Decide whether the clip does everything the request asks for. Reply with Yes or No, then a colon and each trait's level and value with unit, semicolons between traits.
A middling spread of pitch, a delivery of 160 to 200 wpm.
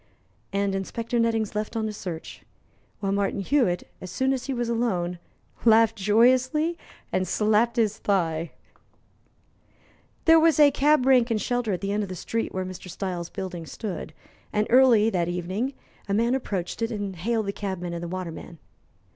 Yes: average, 4.3 semitones; average, 170 wpm